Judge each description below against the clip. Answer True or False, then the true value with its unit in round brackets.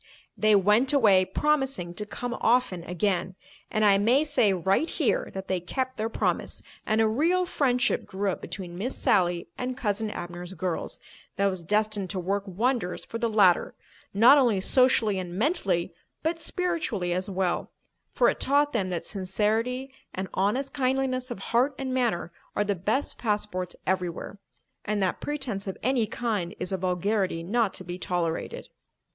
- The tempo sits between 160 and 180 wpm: True (165 wpm)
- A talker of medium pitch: False (210 Hz)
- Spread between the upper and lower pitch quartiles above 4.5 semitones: True (5.2 semitones)